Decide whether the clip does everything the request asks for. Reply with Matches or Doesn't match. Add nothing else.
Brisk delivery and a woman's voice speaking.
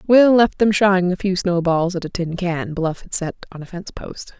Matches